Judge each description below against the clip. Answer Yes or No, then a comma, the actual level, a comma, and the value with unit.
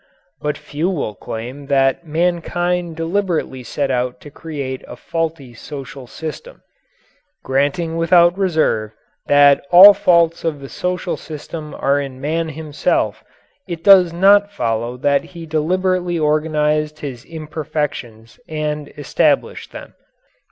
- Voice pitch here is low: No, medium, 155 Hz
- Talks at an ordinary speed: No, slow, 125 wpm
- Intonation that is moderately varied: Yes, average, 3.5 semitones